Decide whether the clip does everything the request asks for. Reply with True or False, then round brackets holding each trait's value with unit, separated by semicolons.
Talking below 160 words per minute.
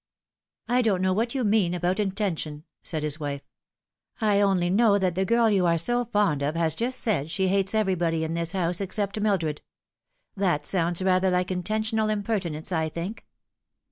False (185 wpm)